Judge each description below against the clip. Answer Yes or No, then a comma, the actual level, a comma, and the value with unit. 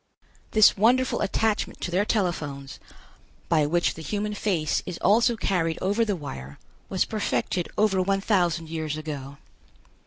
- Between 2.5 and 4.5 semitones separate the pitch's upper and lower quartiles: No, average, 5.0 semitones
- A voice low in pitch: No, medium, 180 Hz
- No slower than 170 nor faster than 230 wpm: No, average, 145 wpm